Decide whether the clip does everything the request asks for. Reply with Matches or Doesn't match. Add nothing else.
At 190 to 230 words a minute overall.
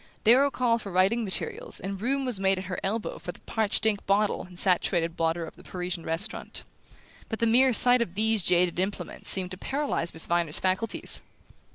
Matches